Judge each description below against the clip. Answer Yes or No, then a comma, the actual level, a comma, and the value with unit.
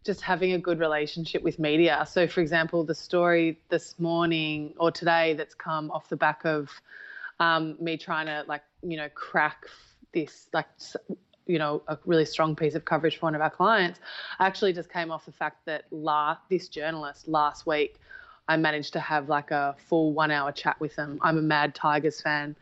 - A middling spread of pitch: No, narrow, 1.9 semitones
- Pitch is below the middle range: No, medium, 160 Hz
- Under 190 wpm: No, average, 200 wpm